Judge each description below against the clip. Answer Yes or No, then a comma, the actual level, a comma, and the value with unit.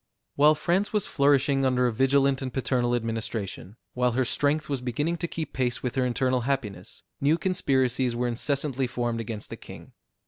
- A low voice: Yes, low, 130 Hz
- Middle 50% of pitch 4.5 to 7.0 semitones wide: No, average, 2.7 semitones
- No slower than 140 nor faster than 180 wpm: Yes, average, 175 wpm